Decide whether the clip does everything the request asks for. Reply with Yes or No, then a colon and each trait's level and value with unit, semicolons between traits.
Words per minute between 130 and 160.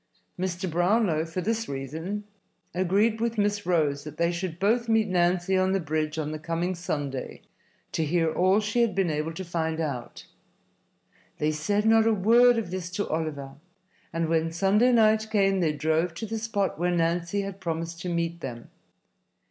No: average, 180 wpm